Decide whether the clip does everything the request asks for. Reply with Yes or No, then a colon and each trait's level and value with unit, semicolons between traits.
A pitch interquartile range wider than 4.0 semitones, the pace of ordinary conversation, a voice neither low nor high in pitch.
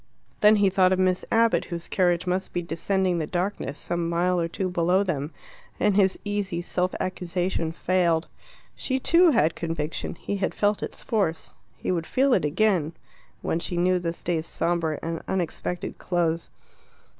No: narrow, 2.4 semitones; average, 170 wpm; medium, 180 Hz